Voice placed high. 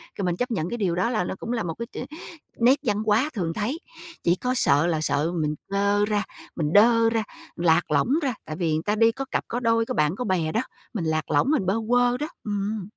Yes: high, 205 Hz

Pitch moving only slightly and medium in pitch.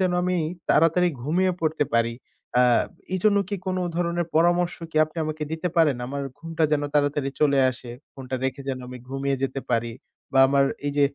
No: average, 4.1 semitones; medium, 150 Hz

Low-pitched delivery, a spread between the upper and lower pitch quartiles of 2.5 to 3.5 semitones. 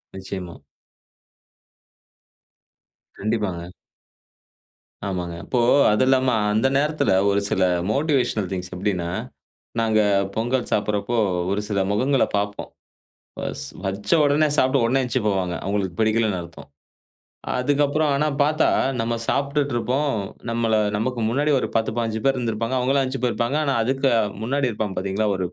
No: low, 115 Hz; average, 4.9 semitones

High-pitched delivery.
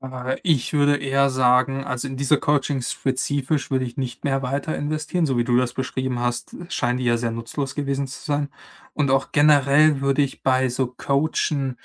No: low, 135 Hz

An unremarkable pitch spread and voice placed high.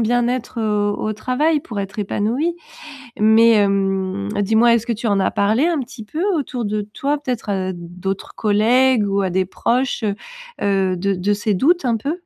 Yes: average, 3.9 semitones; high, 215 Hz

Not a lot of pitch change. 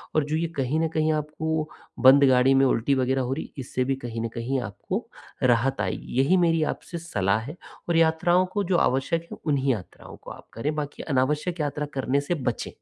No: average, 3.6 semitones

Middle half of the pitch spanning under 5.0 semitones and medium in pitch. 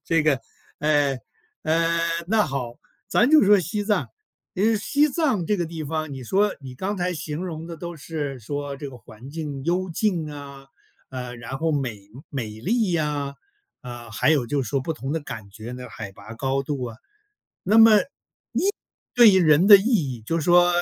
No: average, 5.3 semitones; medium, 155 Hz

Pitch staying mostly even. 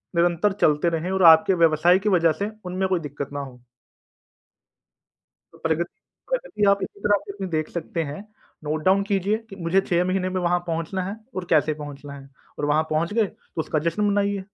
No: average, 3.7 semitones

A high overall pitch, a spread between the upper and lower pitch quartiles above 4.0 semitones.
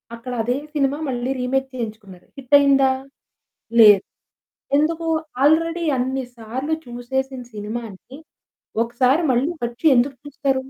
No: very high, 260 Hz; average, 2.8 semitones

